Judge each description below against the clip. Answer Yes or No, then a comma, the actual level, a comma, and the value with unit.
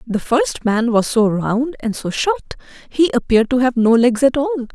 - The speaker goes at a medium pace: No, fast, 215 wpm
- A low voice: No, high, 245 Hz